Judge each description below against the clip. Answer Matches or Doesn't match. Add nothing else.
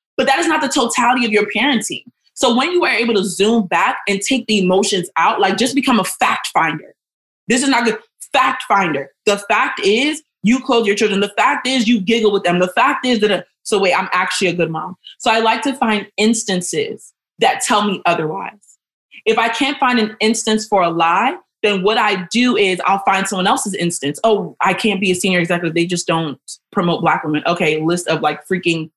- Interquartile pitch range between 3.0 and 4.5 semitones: Doesn't match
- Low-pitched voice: Doesn't match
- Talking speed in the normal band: Doesn't match